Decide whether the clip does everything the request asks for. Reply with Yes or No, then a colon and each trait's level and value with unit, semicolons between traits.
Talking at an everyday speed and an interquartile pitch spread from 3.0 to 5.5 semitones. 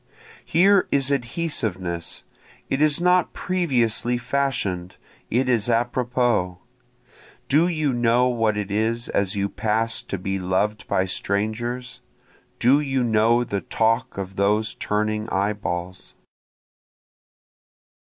No: slow, 115 wpm; average, 4.1 semitones